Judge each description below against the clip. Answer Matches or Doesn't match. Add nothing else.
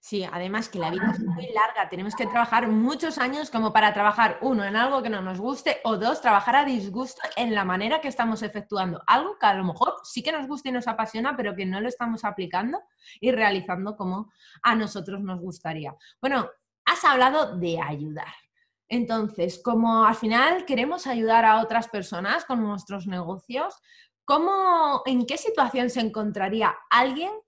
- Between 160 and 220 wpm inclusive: Matches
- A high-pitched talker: Matches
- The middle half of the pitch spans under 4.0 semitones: Doesn't match